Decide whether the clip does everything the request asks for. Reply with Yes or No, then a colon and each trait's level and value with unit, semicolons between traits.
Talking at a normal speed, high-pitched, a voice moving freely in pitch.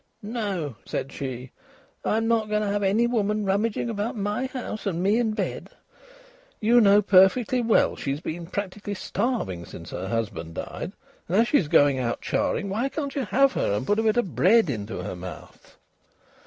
Yes: average, 180 wpm; high, 205 Hz; wide, 7.8 semitones